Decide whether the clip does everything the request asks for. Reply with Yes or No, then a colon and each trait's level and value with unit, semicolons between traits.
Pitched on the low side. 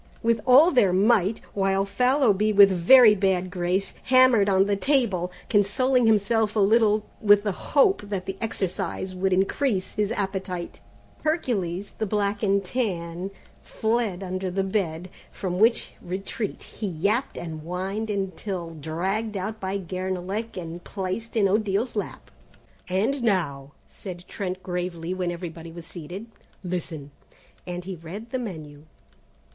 No: high, 195 Hz